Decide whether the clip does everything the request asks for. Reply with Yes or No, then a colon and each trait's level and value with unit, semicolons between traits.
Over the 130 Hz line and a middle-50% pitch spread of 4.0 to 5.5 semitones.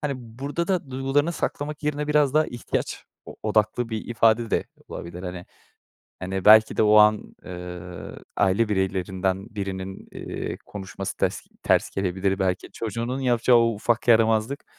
No: low, 110 Hz; average, 4.8 semitones